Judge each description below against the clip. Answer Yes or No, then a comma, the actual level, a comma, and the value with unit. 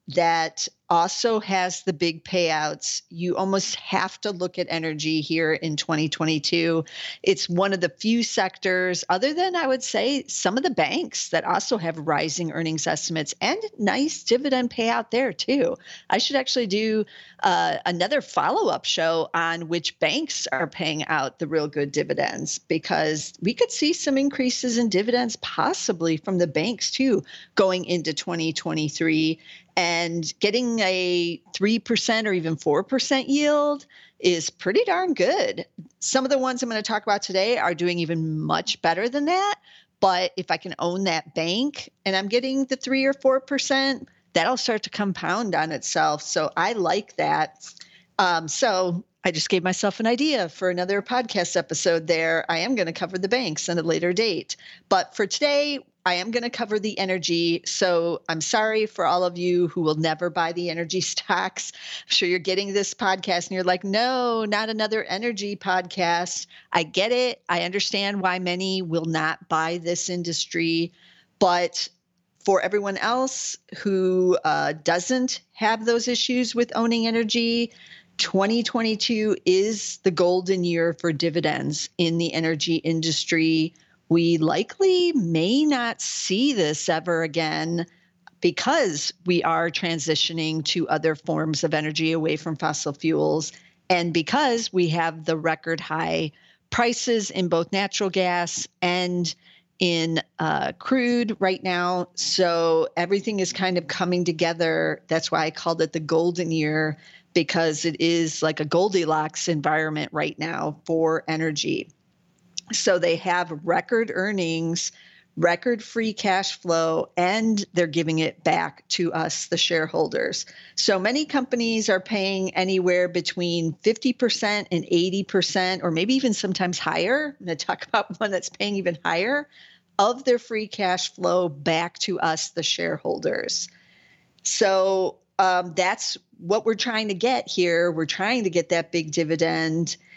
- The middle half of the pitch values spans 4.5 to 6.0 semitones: Yes, average, 4.9 semitones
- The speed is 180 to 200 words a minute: No, average, 155 wpm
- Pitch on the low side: No, medium, 180 Hz